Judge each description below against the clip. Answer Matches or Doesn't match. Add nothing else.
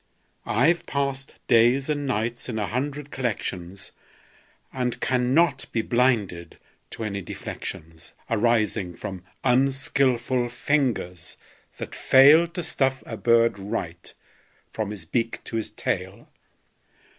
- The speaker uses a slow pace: Matches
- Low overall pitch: Matches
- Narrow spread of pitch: Doesn't match